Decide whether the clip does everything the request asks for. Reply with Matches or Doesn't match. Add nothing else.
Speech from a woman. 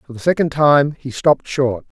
Doesn't match